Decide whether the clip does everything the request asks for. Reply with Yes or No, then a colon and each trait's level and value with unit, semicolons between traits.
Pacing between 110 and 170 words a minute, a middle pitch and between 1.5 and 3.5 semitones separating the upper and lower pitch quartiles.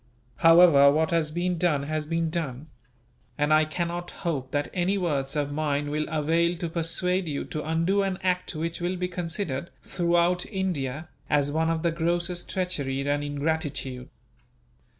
Yes: average, 160 wpm; medium, 165 Hz; average, 3.0 semitones